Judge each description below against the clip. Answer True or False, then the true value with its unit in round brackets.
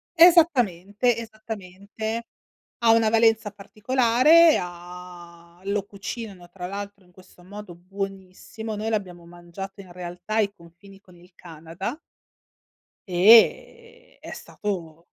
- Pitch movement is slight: False (3.9 semitones)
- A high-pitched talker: True (200 Hz)